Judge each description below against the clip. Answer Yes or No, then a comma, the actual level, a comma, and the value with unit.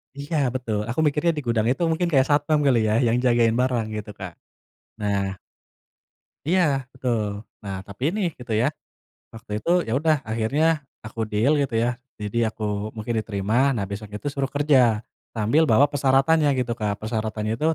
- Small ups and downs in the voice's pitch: No, average, 4.8 semitones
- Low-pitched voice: Yes, low, 115 Hz